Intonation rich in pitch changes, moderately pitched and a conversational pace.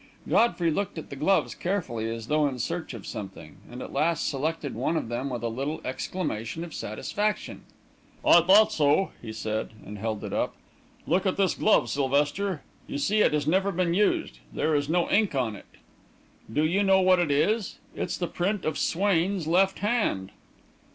Yes: wide, 6.5 semitones; medium, 160 Hz; average, 185 wpm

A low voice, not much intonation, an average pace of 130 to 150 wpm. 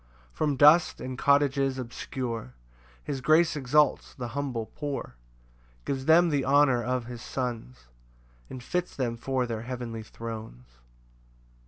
No: low, 130 Hz; average, 3.4 semitones; slow, 135 wpm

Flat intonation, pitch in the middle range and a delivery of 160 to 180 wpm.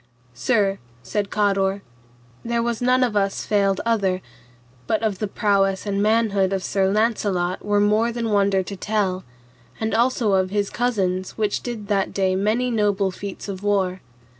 No: narrow, 2.3 semitones; high, 205 Hz; average, 165 wpm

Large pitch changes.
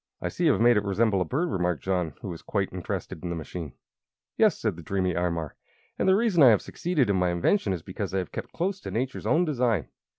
Yes: wide, 7.2 semitones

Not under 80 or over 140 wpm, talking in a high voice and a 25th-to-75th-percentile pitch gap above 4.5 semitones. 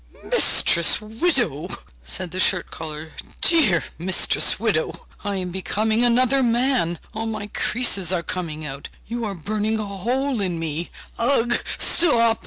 Yes: slow, 135 wpm; high, 205 Hz; wide, 5.6 semitones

